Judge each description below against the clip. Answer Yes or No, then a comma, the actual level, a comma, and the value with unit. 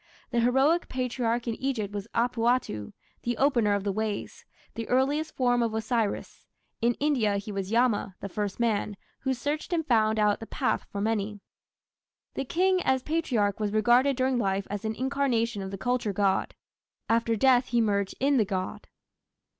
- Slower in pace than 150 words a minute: No, average, 170 wpm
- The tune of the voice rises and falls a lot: No, average, 3.8 semitones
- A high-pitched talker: Yes, high, 230 Hz